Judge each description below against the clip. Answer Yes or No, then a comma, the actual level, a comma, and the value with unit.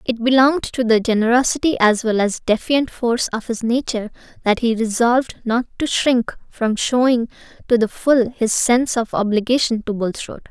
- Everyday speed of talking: Yes, average, 170 wpm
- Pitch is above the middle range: Yes, high, 235 Hz